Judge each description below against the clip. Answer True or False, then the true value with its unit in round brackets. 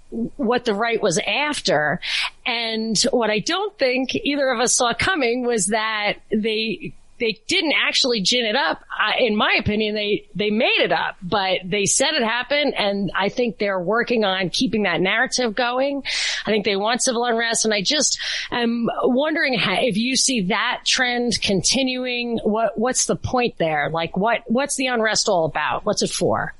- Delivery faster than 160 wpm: True (185 wpm)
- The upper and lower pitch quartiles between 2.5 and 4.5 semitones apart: True (3.2 semitones)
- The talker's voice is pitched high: True (230 Hz)